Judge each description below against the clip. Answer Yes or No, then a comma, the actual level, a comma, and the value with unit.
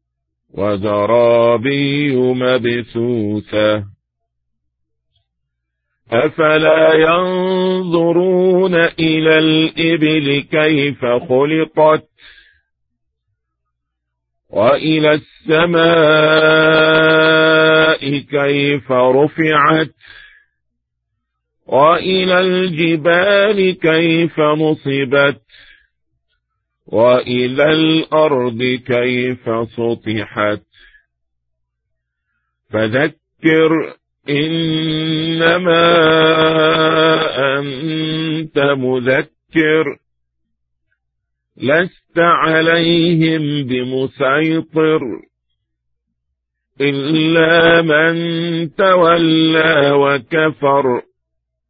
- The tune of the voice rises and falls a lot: Yes, wide, 5.9 semitones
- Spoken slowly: Yes, slow, 35 wpm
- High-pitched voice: No, medium, 145 Hz